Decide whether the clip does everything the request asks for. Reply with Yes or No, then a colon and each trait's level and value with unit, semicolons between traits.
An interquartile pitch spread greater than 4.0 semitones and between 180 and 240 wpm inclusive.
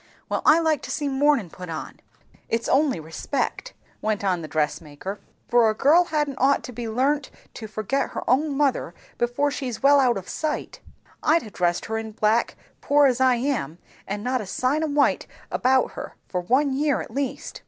Yes: average, 5.1 semitones; average, 200 wpm